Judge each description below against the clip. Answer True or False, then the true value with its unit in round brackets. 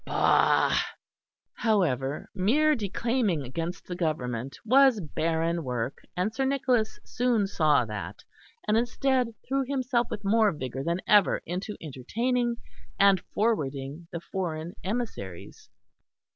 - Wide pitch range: True (7.7 semitones)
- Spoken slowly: True (115 wpm)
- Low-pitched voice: False (190 Hz)